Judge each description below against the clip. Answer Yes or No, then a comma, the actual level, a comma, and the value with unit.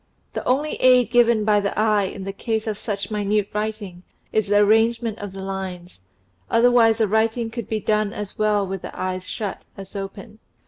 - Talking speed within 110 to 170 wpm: No, average, 190 wpm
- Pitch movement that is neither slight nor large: No, narrow, 2.3 semitones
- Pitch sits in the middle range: No, high, 210 Hz